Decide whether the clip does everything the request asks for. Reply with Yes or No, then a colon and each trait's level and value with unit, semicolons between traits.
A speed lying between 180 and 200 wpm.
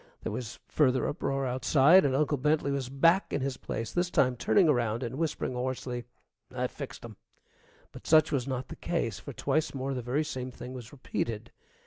Yes: average, 190 wpm